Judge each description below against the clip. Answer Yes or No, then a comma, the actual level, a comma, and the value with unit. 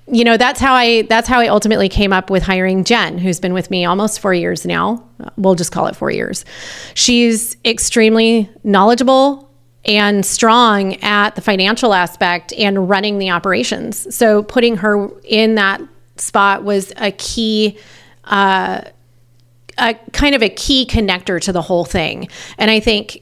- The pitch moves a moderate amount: Yes, average, 3.4 semitones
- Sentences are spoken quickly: No, average, 165 wpm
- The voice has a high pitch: Yes, high, 205 Hz